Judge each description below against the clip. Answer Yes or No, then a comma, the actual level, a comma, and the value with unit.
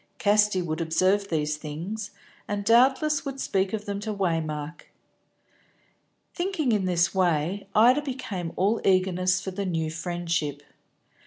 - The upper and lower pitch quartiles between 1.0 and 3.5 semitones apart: No, average, 4.2 semitones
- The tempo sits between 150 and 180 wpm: No, slow, 135 wpm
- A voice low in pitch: No, high, 190 Hz